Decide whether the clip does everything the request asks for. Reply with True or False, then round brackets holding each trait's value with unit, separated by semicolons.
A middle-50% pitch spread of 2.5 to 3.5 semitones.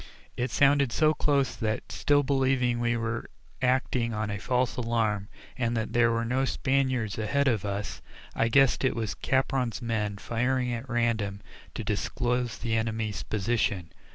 True (2.9 semitones)